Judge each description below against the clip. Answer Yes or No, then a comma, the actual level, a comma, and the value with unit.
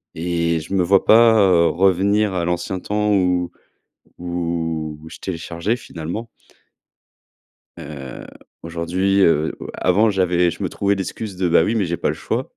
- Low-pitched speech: Yes, very low, 90 Hz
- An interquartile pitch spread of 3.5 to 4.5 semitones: No, average, 2.8 semitones